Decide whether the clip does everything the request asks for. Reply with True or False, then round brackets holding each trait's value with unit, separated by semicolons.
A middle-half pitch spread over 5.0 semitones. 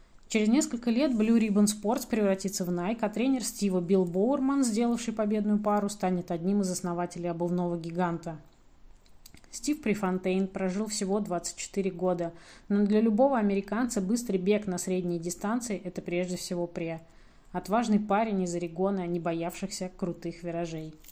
False (3.4 semitones)